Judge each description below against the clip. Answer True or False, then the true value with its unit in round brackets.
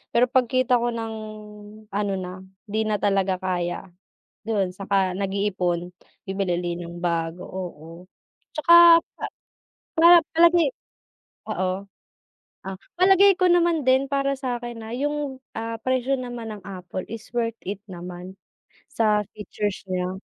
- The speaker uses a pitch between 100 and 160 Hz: False (210 Hz)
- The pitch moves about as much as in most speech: False (5.7 semitones)